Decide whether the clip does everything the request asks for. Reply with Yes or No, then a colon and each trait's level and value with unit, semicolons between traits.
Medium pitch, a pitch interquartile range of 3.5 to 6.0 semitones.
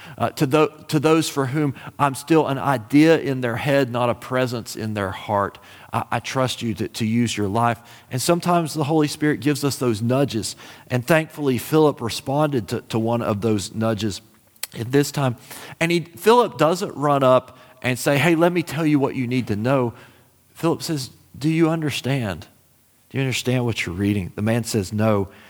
No: low, 130 Hz; average, 4.6 semitones